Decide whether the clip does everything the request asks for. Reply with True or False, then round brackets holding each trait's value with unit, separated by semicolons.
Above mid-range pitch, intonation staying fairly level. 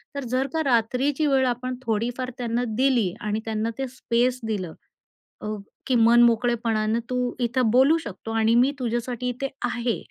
True (240 Hz; 2.2 semitones)